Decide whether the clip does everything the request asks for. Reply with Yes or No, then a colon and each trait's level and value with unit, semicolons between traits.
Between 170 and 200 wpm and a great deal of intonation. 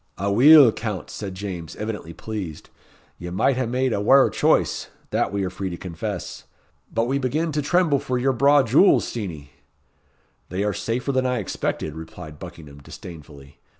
No: average, 160 wpm; wide, 6.9 semitones